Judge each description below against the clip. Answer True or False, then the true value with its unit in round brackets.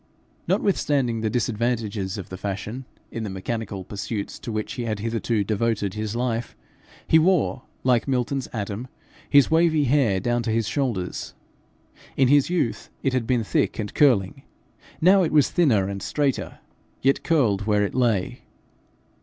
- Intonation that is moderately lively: True (4.6 semitones)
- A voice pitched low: True (115 Hz)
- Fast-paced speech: False (155 wpm)